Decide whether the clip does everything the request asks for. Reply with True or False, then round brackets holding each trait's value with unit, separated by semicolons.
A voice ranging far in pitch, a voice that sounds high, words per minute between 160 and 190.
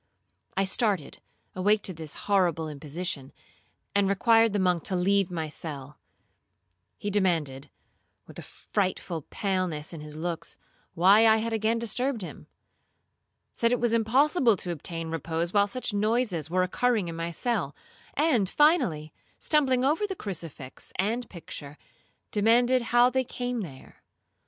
False (5.9 semitones; 195 Hz; 140 wpm)